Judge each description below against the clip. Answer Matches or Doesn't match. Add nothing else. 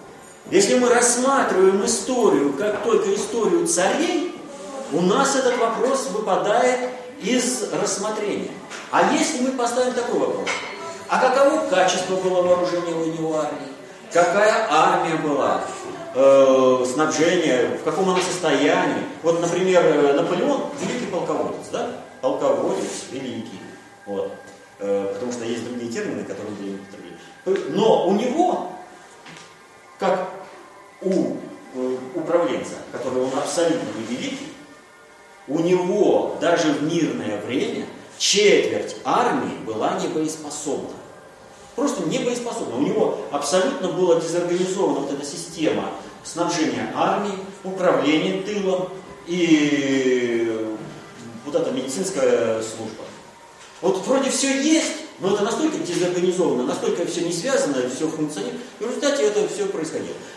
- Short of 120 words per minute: Matches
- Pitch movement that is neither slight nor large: Doesn't match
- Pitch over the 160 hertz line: Matches